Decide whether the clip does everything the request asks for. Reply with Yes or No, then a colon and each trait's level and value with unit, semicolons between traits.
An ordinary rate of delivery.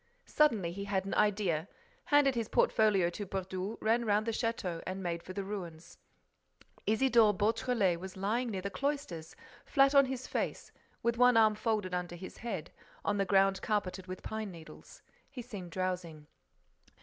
Yes: average, 165 wpm